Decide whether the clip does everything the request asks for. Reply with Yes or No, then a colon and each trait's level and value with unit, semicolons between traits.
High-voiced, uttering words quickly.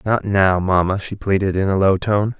No: very low, 95 Hz; fast, 225 wpm